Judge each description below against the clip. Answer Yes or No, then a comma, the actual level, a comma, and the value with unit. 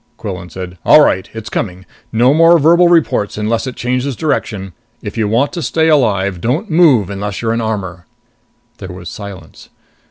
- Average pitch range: No, wide, 6.9 semitones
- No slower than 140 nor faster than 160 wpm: No, average, 170 wpm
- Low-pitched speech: Yes, low, 110 Hz